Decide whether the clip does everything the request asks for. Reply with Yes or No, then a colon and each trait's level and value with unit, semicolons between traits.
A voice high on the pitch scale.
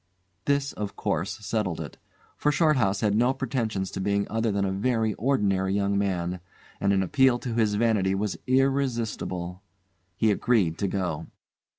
No: low, 105 Hz